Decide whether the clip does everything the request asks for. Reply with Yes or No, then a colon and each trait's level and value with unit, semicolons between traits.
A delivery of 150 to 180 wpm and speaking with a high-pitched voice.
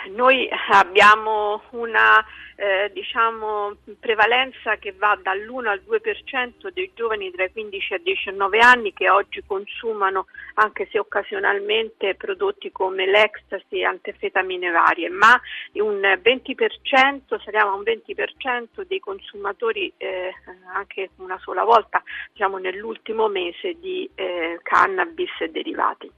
No: average, 125 wpm; high, 235 Hz